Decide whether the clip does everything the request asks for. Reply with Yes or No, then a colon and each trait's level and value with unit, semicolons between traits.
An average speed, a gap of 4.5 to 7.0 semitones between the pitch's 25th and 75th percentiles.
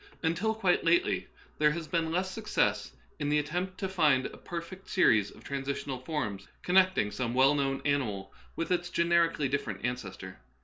Yes: average, 165 wpm; average, 5.3 semitones